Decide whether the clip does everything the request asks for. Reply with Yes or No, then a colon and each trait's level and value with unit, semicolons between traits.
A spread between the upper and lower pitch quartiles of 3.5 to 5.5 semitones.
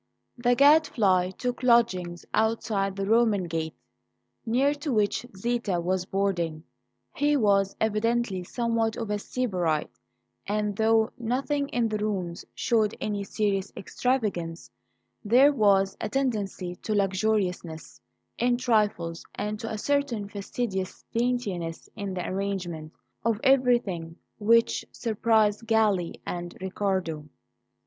Yes: average, 3.9 semitones